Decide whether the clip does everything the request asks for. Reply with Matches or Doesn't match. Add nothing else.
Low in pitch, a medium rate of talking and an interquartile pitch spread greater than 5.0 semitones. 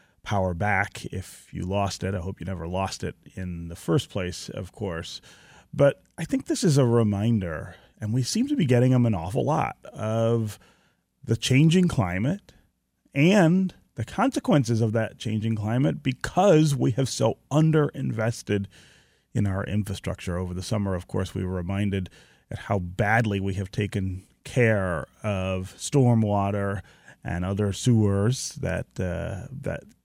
Matches